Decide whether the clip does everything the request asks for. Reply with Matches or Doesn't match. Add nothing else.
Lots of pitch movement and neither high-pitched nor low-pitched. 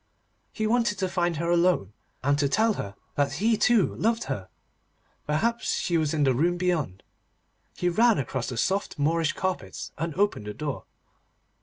Matches